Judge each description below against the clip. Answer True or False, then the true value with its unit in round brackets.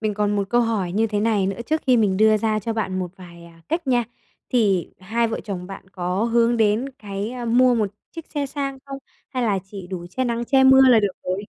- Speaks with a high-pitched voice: True (220 Hz)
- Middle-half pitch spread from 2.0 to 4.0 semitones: True (3.7 semitones)